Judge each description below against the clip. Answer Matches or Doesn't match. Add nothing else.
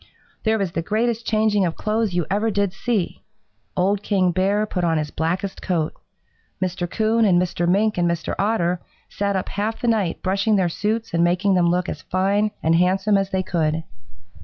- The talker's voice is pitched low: Doesn't match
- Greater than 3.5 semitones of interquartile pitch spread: Doesn't match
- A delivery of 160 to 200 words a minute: Matches